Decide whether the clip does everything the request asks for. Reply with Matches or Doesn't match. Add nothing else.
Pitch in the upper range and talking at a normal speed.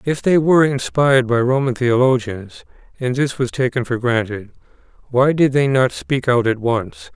Doesn't match